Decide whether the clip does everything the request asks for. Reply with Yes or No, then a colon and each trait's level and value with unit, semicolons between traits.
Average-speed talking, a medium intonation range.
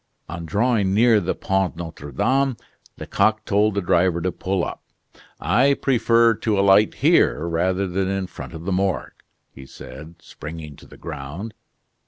Yes: average, 160 wpm; average, 4.2 semitones